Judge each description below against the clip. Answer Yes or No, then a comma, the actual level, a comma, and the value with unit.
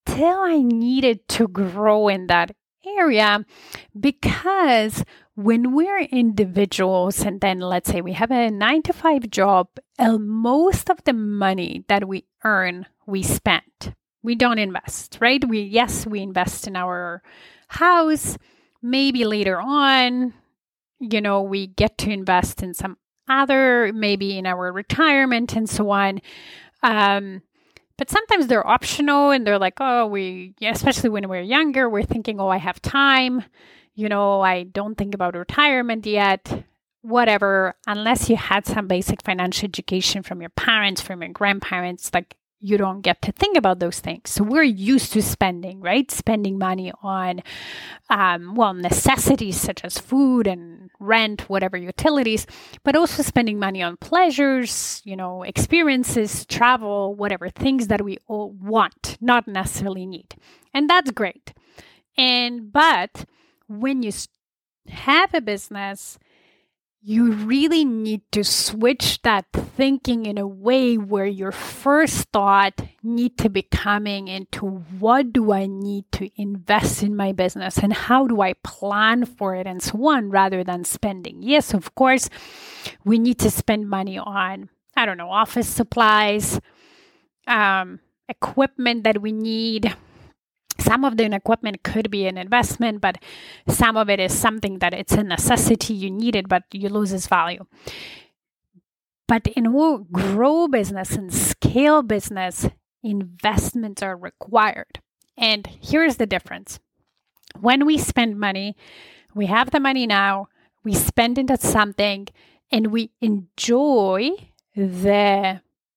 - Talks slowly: No, average, 145 wpm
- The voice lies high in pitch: Yes, high, 210 Hz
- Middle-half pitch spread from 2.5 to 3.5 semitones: No, average, 4.2 semitones